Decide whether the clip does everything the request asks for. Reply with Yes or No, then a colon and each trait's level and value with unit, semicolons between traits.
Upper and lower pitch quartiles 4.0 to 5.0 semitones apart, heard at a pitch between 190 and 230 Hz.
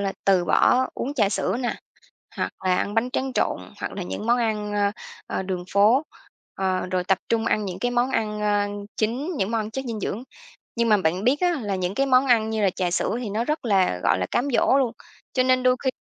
Yes: average, 4.3 semitones; high, 215 Hz